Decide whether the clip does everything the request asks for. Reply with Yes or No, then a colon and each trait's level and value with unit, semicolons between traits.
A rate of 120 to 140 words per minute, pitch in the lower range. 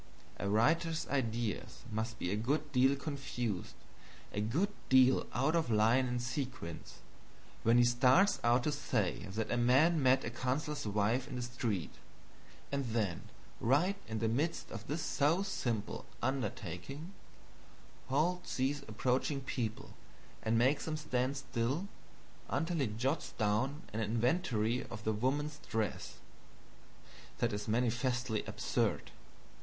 Yes: slow, 135 wpm; low, 125 Hz